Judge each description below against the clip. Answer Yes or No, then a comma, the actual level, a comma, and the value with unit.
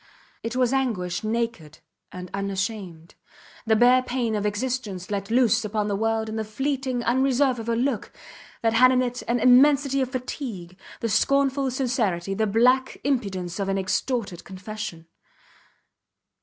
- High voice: Yes, high, 230 Hz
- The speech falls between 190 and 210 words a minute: No, average, 150 wpm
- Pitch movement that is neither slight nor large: Yes, average, 4.4 semitones